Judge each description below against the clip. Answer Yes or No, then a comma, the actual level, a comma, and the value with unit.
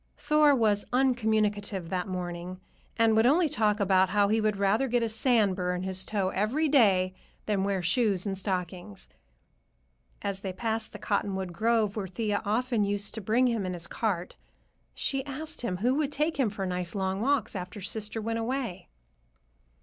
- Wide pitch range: No, average, 3.6 semitones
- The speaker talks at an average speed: Yes, average, 180 wpm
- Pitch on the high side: Yes, high, 210 Hz